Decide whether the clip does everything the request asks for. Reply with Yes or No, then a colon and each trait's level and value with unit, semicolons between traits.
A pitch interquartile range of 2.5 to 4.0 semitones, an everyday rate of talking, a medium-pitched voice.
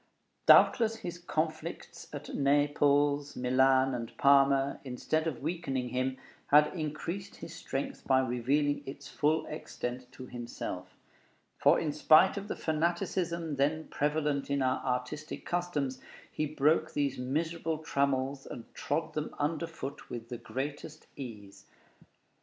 No: average, 3.1 semitones; slow, 130 wpm; medium, 145 Hz